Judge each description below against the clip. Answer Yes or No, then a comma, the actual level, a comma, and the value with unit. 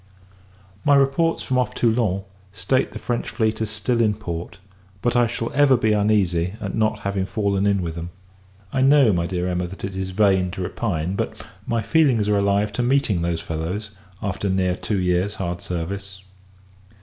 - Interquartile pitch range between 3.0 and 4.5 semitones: Yes, average, 3.8 semitones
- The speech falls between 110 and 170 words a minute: No, average, 185 wpm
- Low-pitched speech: Yes, low, 100 Hz